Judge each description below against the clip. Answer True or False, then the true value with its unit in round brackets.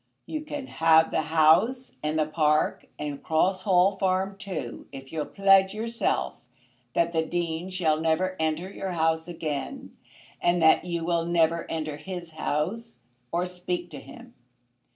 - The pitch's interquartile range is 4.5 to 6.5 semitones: False (2.9 semitones)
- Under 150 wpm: False (155 wpm)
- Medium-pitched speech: True (170 Hz)